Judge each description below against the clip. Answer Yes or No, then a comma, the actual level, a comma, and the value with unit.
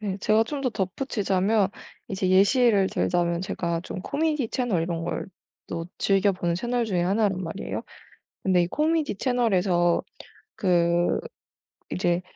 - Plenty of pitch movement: No, average, 4.4 semitones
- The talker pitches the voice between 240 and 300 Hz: No, high, 190 Hz